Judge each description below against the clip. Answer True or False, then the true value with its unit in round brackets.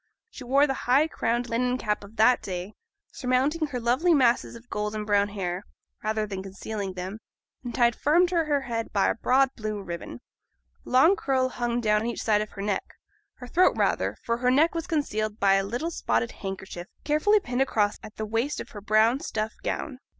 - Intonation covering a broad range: False (4.2 semitones)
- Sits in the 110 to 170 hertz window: False (235 Hz)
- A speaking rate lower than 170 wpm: False (200 wpm)